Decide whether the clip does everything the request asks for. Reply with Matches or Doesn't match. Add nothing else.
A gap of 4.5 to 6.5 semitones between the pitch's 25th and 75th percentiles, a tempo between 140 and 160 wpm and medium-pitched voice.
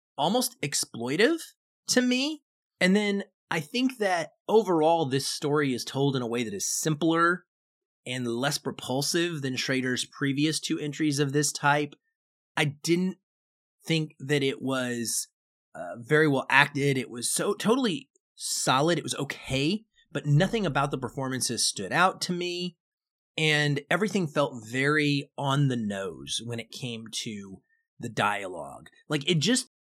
Matches